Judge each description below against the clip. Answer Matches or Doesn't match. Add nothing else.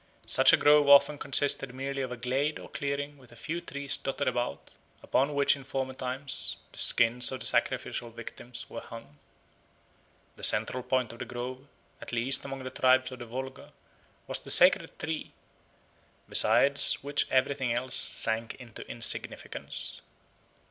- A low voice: Matches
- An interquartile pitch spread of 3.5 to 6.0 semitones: Doesn't match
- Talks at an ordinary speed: Matches